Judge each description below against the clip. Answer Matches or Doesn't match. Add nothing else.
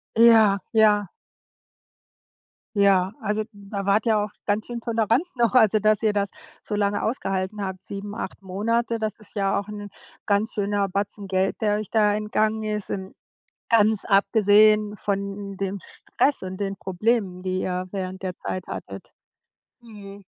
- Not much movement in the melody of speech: Matches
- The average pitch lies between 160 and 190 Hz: Doesn't match